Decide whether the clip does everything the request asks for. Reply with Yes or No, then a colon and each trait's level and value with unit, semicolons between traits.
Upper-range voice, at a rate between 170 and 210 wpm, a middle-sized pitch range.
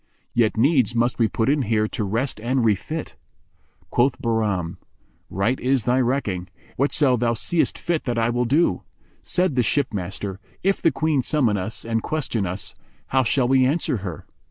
No: low, 120 Hz; average, 180 wpm; average, 4.2 semitones